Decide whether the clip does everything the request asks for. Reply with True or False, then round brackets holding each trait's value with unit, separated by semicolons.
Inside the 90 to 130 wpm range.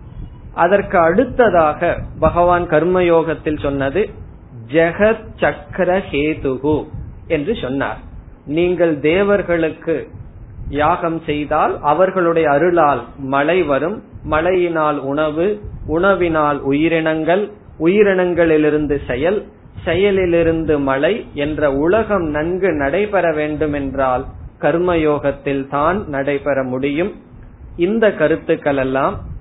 False (80 wpm)